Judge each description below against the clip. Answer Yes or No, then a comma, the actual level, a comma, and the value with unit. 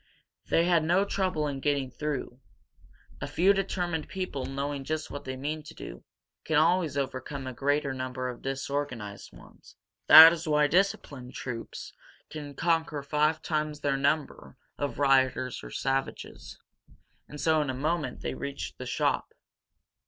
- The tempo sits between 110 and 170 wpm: Yes, average, 150 wpm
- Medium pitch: Yes, medium, 145 Hz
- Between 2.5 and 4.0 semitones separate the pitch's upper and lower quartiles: Yes, average, 2.9 semitones